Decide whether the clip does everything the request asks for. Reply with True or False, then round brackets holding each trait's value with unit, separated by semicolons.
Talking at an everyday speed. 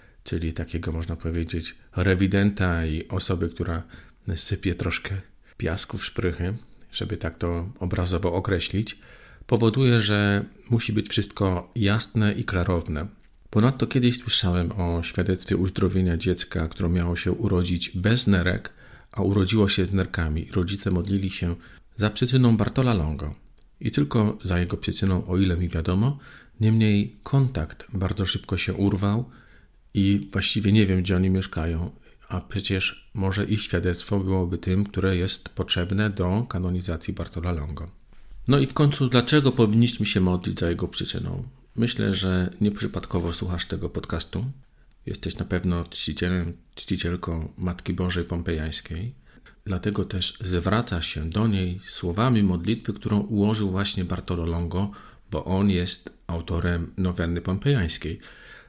True (135 wpm)